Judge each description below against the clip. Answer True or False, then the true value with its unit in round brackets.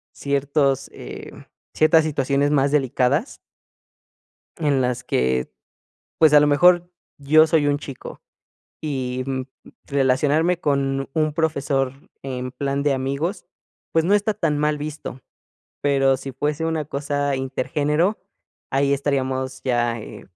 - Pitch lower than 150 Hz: True (140 Hz)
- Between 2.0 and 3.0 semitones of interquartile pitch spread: True (2.4 semitones)